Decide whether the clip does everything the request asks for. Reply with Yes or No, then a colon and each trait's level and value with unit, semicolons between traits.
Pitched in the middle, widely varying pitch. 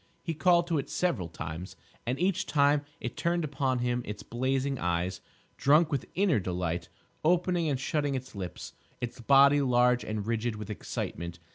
No: low, 130 Hz; wide, 6.0 semitones